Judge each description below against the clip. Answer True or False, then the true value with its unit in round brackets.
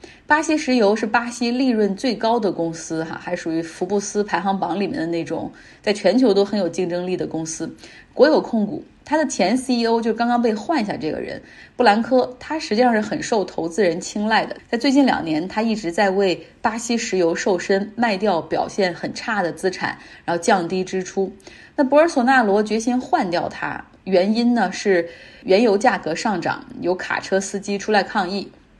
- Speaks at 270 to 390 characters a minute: True (285 characters per minute)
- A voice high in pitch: True (205 Hz)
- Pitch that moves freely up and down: False (4.7 semitones)